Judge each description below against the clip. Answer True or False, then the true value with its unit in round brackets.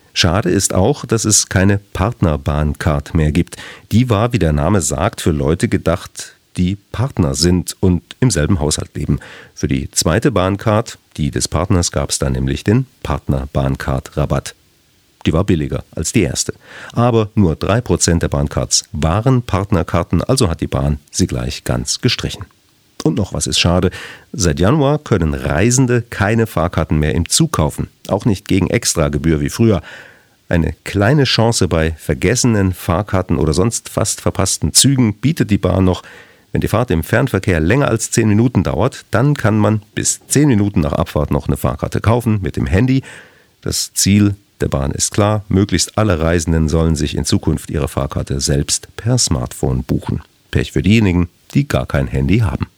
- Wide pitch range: True (6.0 semitones)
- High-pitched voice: False (95 Hz)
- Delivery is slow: False (170 wpm)